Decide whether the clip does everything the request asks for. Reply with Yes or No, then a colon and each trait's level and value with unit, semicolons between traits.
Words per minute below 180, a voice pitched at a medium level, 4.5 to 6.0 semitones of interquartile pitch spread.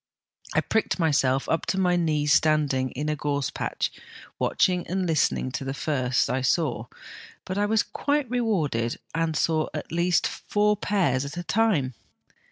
Yes: average, 165 wpm; medium, 160 Hz; wide, 5.4 semitones